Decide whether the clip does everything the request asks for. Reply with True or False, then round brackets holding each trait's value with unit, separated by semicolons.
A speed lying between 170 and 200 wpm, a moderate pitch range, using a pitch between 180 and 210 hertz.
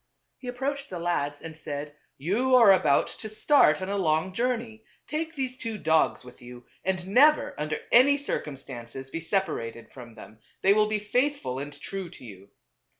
False (180 wpm; 9.0 semitones; 185 Hz)